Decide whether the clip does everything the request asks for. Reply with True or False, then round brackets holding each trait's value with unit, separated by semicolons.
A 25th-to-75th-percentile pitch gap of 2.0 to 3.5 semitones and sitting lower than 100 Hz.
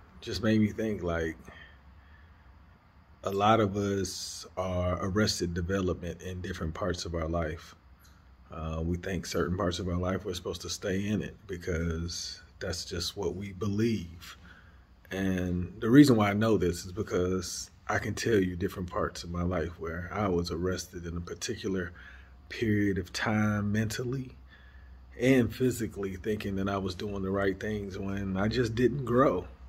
True (3.0 semitones; 90 Hz)